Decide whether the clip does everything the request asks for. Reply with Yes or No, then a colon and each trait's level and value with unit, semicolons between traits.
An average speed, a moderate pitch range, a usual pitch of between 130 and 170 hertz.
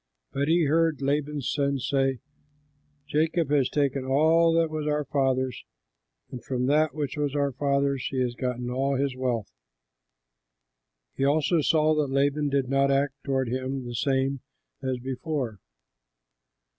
No: average, 145 wpm; narrow, 2.2 semitones; medium, 140 Hz